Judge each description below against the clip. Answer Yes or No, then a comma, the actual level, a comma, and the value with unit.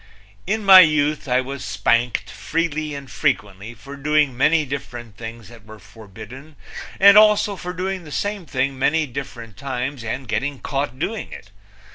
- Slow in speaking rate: No, average, 160 wpm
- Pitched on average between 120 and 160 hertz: Yes, medium, 140 Hz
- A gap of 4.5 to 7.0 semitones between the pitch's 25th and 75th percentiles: Yes, average, 4.9 semitones